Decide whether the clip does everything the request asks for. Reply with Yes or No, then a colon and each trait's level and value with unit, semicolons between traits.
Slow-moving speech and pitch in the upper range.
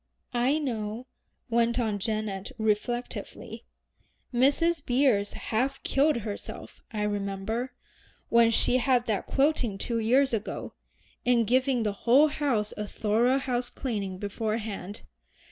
Yes: slow, 120 wpm; high, 235 Hz